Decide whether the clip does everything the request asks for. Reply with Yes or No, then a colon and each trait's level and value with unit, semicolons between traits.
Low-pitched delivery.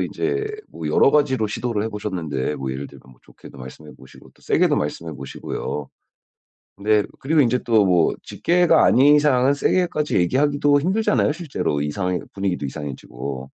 Yes: low, 105 Hz